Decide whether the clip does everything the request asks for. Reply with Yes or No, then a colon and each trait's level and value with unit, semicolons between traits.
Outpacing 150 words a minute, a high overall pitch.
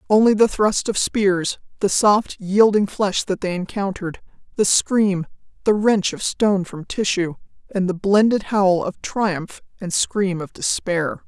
Yes: average, 160 wpm; high, 195 Hz